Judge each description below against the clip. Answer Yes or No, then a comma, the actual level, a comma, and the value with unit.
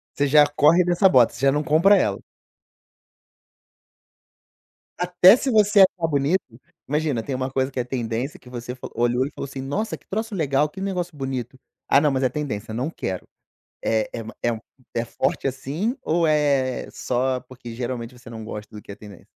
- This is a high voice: No, low, 135 Hz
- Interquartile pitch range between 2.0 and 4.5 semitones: No, average, 4.9 semitones